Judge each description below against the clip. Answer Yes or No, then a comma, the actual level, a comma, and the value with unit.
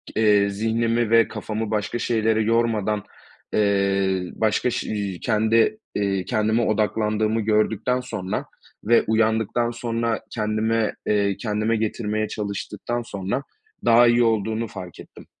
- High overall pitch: No, low, 110 Hz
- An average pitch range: No, narrow, 1.7 semitones